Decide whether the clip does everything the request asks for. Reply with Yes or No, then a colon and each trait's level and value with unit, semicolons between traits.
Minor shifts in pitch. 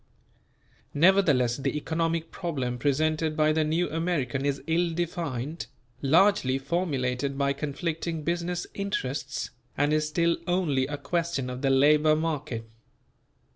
No: average, 3.5 semitones